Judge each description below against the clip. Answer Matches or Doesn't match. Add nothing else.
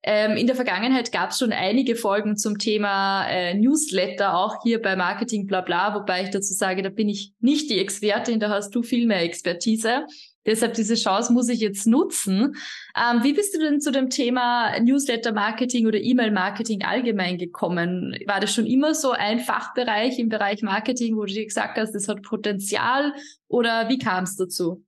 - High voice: Matches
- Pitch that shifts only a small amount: Doesn't match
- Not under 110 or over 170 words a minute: Doesn't match